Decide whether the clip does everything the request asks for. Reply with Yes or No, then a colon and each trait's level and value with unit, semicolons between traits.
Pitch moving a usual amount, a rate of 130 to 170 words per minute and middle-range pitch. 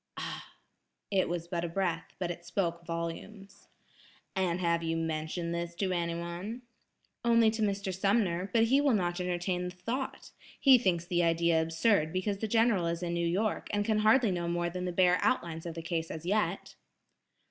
No: average, 3.2 semitones; average, 185 wpm; medium, 180 Hz